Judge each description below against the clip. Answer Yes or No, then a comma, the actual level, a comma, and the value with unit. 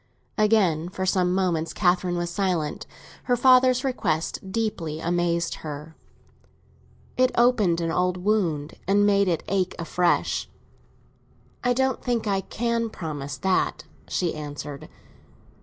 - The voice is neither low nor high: Yes, medium, 180 Hz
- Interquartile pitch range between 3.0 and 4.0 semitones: No, average, 4.6 semitones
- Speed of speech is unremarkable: No, slow, 125 wpm